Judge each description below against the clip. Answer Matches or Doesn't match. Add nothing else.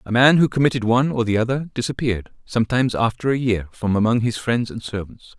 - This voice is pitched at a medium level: Doesn't match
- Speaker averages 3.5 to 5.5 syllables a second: Doesn't match